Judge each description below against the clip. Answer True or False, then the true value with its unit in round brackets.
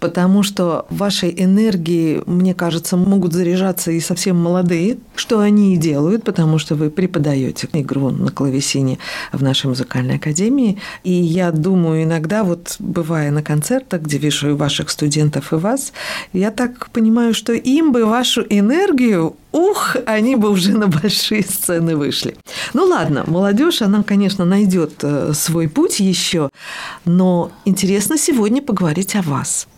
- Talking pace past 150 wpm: False (145 wpm)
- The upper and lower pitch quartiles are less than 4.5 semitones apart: False (4.9 semitones)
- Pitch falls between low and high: True (180 Hz)